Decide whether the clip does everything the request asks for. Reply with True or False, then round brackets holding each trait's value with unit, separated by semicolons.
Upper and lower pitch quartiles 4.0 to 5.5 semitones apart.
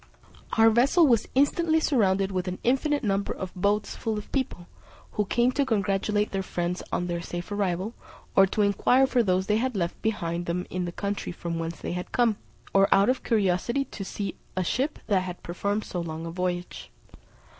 True (4.3 semitones)